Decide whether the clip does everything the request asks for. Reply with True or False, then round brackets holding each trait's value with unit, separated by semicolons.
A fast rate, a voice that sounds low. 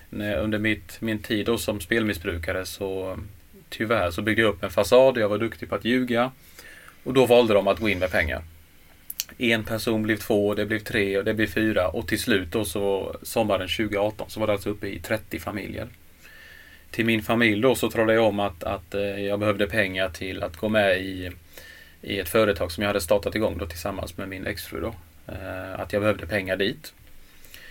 True (205 wpm; 105 Hz)